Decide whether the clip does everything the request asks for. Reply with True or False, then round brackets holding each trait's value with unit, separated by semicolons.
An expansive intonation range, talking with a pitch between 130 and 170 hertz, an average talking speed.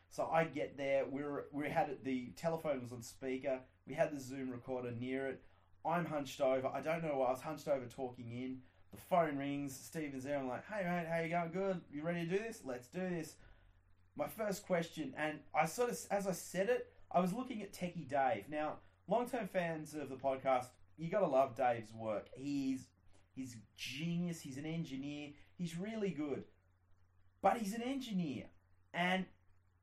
True (5.7 semitones; 140 Hz; 195 wpm)